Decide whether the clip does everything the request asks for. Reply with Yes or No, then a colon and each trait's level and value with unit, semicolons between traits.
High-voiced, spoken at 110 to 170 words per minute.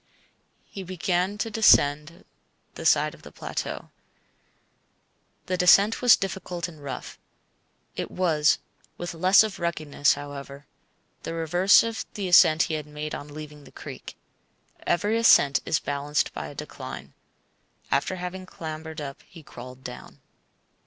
No: medium, 165 Hz; average, 140 wpm